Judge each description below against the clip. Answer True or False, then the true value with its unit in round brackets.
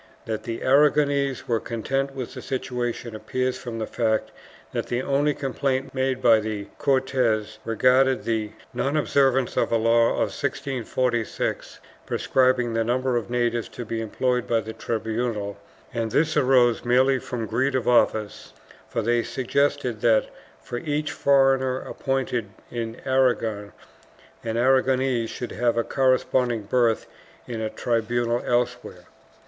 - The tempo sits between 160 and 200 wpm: False (140 wpm)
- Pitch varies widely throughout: False (2.5 semitones)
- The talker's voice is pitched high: False (120 Hz)